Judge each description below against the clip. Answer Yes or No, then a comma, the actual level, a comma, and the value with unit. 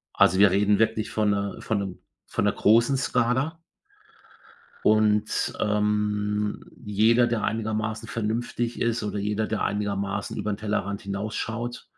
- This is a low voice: Yes, low, 105 Hz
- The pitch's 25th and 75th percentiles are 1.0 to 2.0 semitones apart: Yes, narrow, 1.7 semitones